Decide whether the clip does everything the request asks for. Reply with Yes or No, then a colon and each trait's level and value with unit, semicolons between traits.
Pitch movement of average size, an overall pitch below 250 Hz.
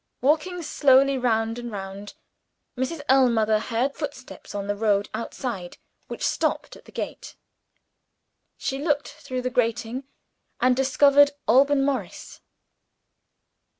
No: average, 3.8 semitones; very high, 255 Hz